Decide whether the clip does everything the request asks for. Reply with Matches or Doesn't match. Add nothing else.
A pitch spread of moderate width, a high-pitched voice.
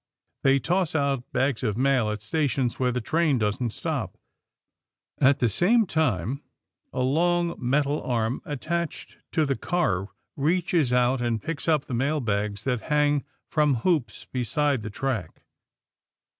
Doesn't match